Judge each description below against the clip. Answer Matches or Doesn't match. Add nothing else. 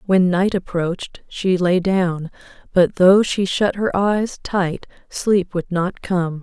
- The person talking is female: Matches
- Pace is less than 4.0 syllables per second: Matches